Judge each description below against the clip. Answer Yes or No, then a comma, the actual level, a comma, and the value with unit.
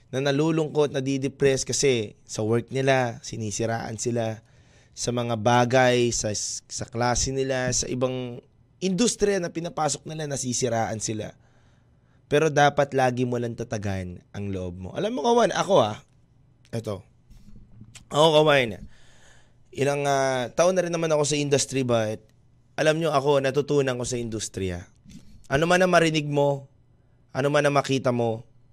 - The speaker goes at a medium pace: Yes, average, 140 wpm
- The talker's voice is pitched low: Yes, low, 125 Hz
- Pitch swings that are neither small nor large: Yes, average, 3.8 semitones